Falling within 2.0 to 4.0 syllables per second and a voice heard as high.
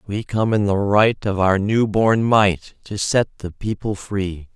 No: 3.7 syllables/s; low, 100 Hz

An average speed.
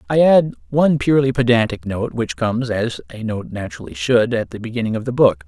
No: fast, 210 wpm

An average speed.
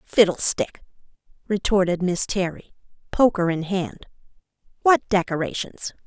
No: slow, 90 wpm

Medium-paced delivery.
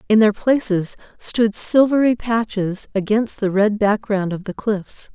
Yes: average, 150 wpm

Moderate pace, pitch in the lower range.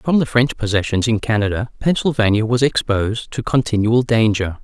Yes: average, 155 wpm; low, 115 Hz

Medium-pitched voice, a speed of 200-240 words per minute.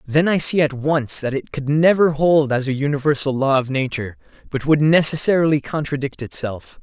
No: medium, 145 Hz; average, 185 wpm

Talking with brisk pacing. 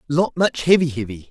No: average, 185 wpm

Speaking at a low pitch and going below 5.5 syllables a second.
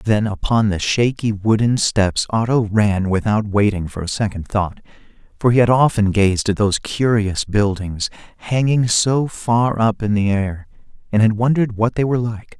Yes: low, 110 Hz; 4.6 syllables/s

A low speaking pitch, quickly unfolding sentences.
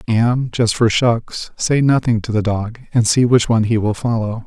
Yes: low, 115 Hz; fast, 215 wpm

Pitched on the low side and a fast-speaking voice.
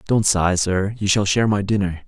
Yes: low, 100 Hz; fast, 230 wpm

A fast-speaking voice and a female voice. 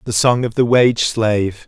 No: fast, 215 wpm; male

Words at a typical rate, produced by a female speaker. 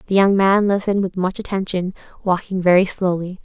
Yes: average, 175 wpm; female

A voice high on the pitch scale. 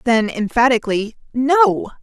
Yes: high, 240 Hz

